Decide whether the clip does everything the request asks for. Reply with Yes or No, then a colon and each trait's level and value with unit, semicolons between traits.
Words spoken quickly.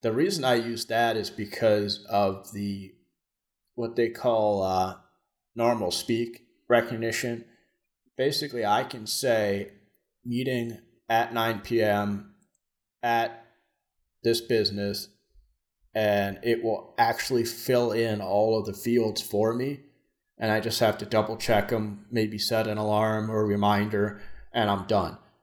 No: slow, 135 wpm